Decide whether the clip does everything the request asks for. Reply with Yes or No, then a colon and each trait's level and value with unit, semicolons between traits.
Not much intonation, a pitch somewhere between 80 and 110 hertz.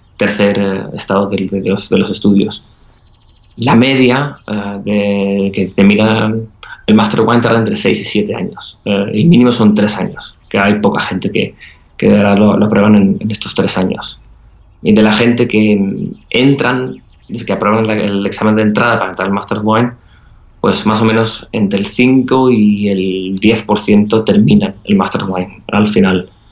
Yes: narrow, 2.1 semitones; low, 105 Hz